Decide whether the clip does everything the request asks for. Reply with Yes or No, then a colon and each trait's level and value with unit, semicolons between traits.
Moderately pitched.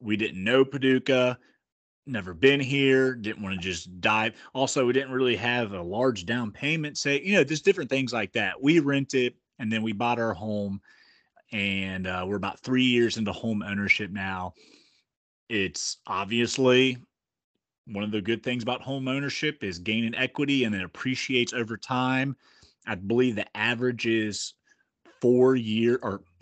No: low, 120 Hz